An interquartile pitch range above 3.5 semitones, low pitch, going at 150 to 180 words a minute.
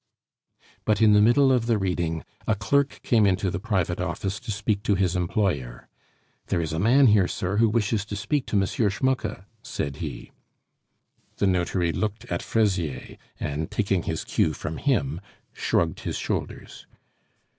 Yes: average, 4.0 semitones; low, 100 Hz; average, 165 wpm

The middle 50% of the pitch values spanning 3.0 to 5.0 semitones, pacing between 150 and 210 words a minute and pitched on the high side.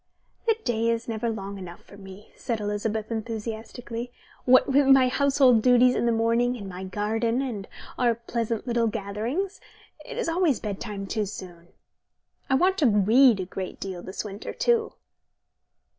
Yes: average, 3.4 semitones; average, 160 wpm; high, 230 Hz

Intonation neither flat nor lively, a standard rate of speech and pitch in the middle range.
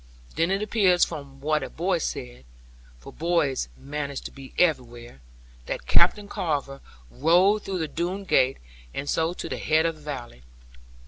Yes: average, 4.4 semitones; average, 165 wpm; medium, 155 Hz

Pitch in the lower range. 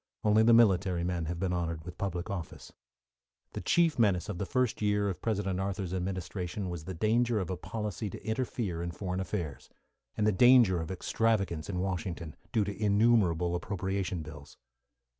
Yes: very low, 95 Hz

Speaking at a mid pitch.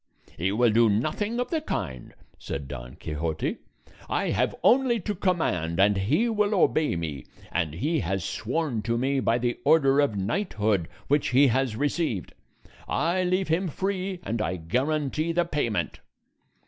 No: low, 130 Hz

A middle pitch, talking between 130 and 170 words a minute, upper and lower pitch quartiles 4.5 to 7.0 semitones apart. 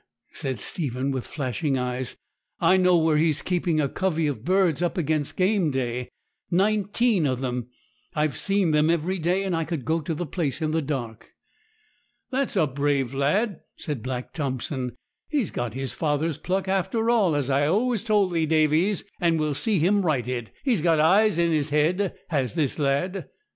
No: medium, 160 Hz; average, 180 wpm; average, 5.1 semitones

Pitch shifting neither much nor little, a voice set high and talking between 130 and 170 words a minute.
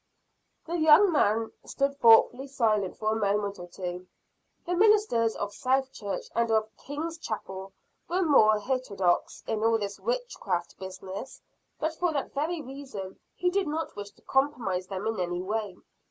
No: wide, 6.8 semitones; high, 225 Hz; average, 160 wpm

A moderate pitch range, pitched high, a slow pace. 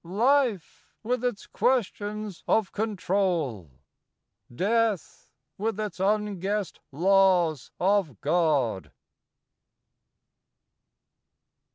Yes: average, 4.0 semitones; high, 195 Hz; slow, 65 wpm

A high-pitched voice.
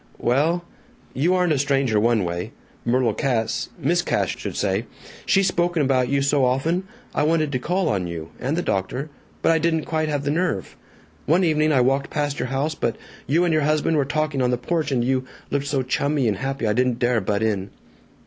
No: medium, 140 Hz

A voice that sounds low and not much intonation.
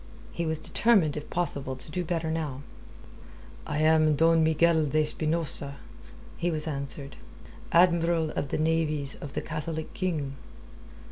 No: medium, 155 Hz; narrow, 2.0 semitones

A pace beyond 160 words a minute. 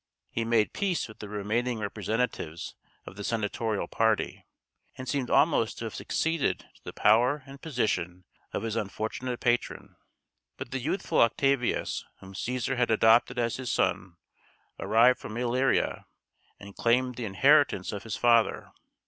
No: average, 150 wpm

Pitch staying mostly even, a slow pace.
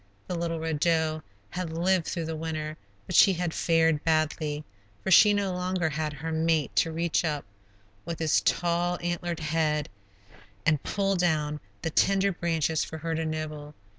No: narrow, 1.9 semitones; average, 165 wpm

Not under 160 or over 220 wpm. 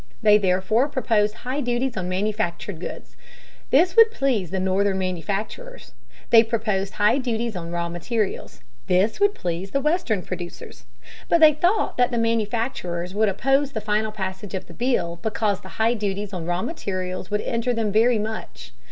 Yes: average, 170 wpm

